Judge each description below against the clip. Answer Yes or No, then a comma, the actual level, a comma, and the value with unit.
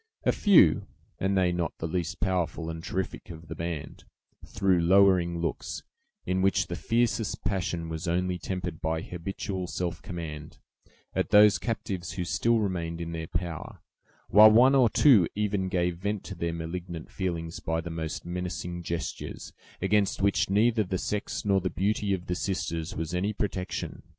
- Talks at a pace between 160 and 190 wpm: Yes, average, 165 wpm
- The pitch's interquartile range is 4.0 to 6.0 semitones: No, average, 2.8 semitones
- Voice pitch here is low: Yes, very low, 90 Hz